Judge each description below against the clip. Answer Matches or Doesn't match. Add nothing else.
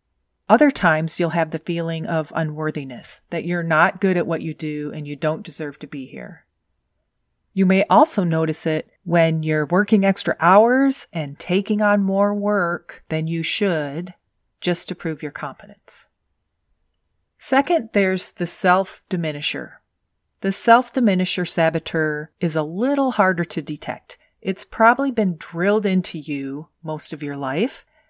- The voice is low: Doesn't match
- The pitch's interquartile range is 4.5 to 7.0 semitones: Doesn't match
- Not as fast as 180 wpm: Matches